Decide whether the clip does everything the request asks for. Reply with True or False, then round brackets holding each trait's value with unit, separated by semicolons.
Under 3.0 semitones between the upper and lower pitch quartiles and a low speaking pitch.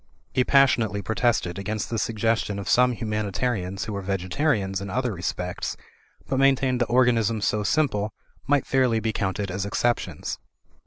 False (4.0 semitones; 110 Hz)